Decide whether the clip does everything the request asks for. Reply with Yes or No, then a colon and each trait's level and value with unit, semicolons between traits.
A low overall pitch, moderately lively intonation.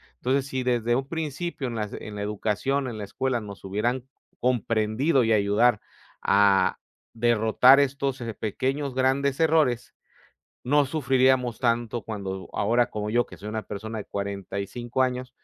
Yes: low, 120 Hz; average, 3.8 semitones